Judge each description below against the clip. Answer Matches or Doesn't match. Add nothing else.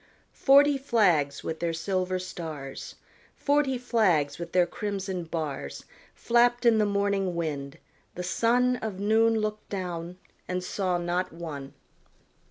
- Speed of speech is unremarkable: Doesn't match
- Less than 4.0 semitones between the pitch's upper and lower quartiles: Doesn't match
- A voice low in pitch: Doesn't match